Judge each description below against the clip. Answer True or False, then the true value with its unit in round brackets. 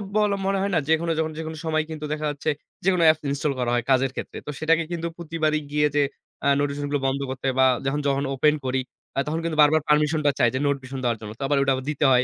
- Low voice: False (150 Hz)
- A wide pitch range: False (2.7 semitones)